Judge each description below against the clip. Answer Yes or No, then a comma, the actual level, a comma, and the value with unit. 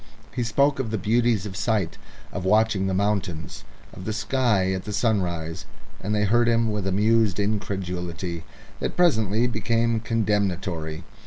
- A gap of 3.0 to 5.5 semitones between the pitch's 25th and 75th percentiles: Yes, average, 3.4 semitones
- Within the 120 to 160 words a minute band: Yes, average, 150 wpm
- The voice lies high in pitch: No, low, 105 Hz